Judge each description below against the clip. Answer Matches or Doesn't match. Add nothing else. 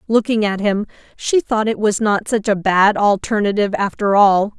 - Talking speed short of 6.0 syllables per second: Matches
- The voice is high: Matches